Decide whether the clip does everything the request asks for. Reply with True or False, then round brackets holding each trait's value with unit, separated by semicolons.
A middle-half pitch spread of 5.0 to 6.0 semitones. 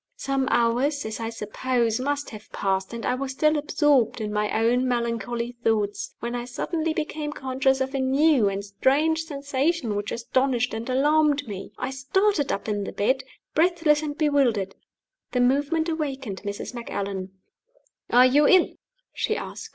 False (4.2 semitones)